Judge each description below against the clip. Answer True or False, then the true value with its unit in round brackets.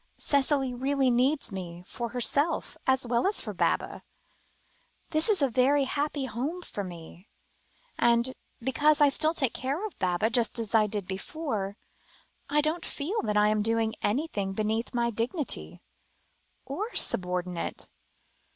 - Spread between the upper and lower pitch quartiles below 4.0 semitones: False (5.4 semitones)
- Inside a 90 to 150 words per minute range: True (140 wpm)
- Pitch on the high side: True (245 Hz)